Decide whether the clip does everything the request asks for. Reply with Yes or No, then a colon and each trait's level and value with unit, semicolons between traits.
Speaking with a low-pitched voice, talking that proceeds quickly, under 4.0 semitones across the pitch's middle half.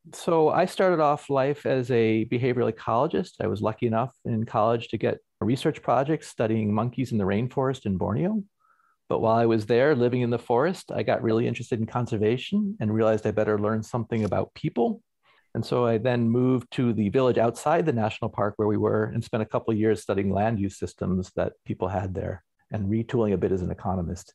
Yes: low, 115 Hz; fast, 210 wpm; average, 3.0 semitones